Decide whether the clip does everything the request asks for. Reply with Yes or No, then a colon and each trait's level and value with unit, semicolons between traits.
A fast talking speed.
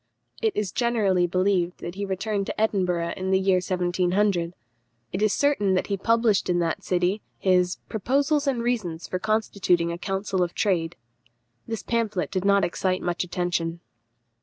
No: average, 160 wpm